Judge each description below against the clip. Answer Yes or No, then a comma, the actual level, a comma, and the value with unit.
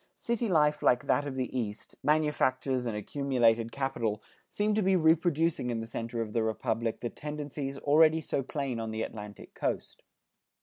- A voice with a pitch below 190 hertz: Yes, low, 135 Hz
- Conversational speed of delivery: Yes, average, 170 wpm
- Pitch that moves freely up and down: No, average, 4.8 semitones